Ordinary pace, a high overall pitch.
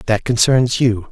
No: average, 160 wpm; low, 115 Hz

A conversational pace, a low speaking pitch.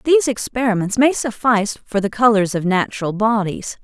No: average, 155 wpm; high, 220 Hz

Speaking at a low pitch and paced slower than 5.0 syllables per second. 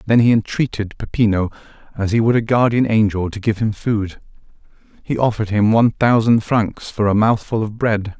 No: low, 110 Hz; 5.3 syllables/s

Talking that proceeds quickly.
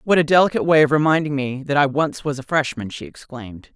Yes: fast, 240 wpm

